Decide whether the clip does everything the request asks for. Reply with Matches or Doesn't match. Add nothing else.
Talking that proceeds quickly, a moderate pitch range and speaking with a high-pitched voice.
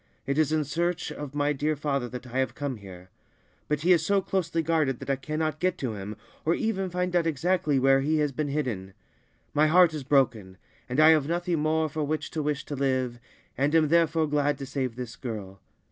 Doesn't match